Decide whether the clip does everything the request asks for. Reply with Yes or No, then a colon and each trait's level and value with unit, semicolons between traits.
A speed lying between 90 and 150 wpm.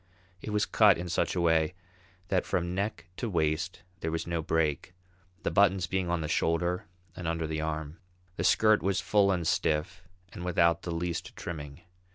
No: average, 185 wpm